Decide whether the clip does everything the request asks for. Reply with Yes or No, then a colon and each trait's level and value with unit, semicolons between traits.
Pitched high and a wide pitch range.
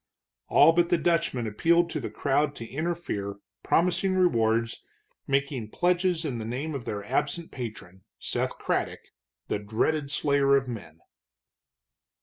No: medium, 140 Hz; wide, 6.9 semitones